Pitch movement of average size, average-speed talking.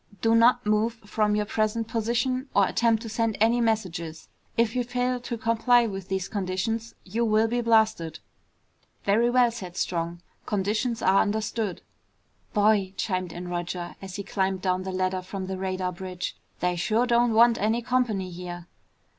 Yes: average, 3.7 semitones; average, 165 wpm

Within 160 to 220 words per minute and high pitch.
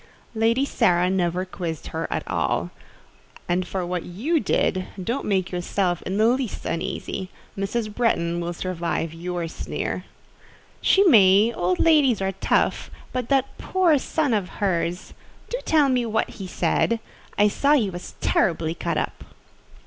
No: average, 150 wpm; high, 195 Hz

